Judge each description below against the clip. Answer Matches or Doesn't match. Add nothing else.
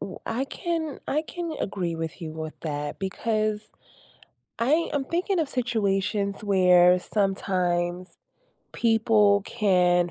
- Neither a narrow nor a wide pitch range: Matches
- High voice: Matches